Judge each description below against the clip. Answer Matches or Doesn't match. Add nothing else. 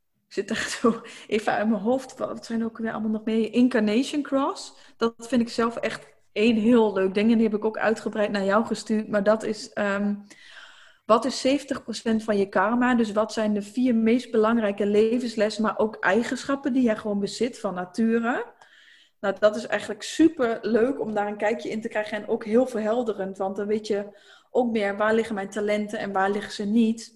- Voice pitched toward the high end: Matches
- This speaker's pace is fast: Matches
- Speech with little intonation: Matches